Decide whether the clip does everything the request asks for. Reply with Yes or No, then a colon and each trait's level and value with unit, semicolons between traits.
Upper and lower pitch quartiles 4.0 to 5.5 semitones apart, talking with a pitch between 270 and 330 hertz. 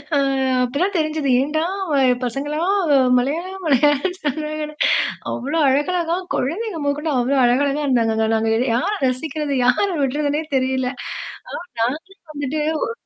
No: average, 3.4 semitones; very high, 290 Hz